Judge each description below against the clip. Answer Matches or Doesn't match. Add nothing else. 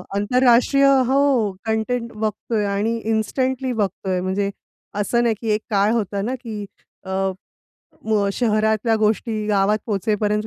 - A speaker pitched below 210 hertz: Doesn't match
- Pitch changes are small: Matches